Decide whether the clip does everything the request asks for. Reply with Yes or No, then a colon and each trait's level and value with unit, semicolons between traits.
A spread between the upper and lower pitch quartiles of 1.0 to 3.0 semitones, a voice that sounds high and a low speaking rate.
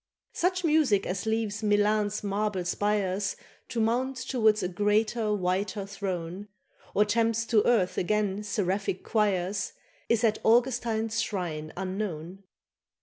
Yes: average, 2.7 semitones; high, 210 Hz; slow, 120 wpm